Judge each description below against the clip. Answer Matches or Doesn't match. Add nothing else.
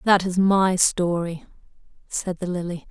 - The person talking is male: Doesn't match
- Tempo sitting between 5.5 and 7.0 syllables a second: Doesn't match